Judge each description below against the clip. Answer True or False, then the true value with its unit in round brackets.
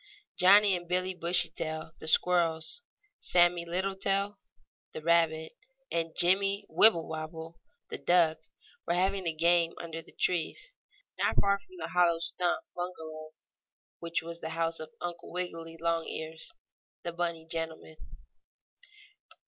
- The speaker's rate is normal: False (125 wpm)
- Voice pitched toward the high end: False (170 Hz)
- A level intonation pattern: True (1.8 semitones)